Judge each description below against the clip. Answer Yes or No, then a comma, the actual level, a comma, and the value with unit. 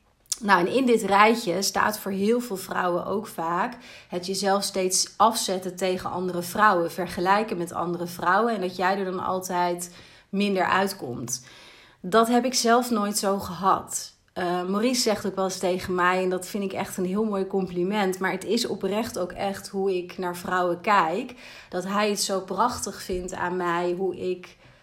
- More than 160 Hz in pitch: Yes, high, 190 Hz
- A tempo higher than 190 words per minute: No, average, 185 wpm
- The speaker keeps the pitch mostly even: Yes, narrow, 2.2 semitones